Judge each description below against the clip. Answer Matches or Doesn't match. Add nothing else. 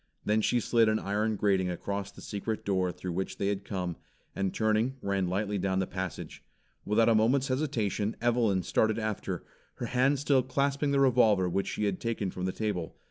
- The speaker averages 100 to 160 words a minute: Doesn't match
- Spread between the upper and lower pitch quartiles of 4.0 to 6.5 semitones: Doesn't match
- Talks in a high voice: Doesn't match